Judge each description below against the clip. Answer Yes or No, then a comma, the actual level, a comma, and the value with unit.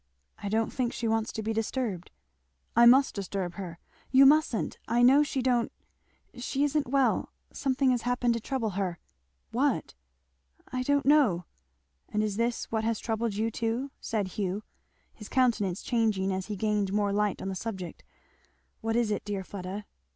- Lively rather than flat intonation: No, average, 3.7 semitones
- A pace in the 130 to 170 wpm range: No, average, 180 wpm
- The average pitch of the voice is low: No, high, 225 Hz